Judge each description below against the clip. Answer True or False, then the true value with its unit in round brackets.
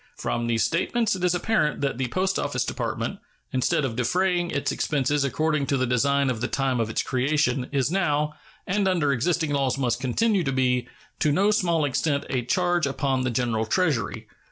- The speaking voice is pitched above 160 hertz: False (140 Hz)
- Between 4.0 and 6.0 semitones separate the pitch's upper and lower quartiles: True (5.3 semitones)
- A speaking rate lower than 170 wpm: False (190 wpm)